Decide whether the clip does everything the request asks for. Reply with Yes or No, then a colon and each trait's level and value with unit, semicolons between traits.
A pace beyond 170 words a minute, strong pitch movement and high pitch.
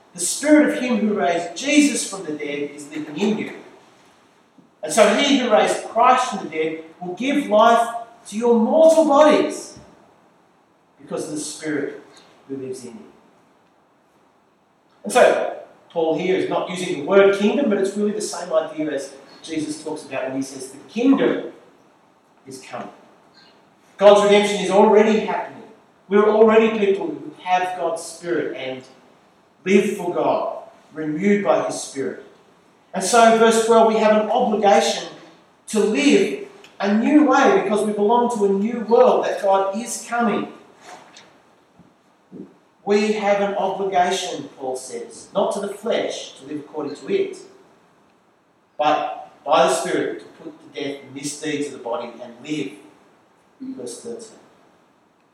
No: average, 155 wpm; wide, 6.2 semitones; high, 205 Hz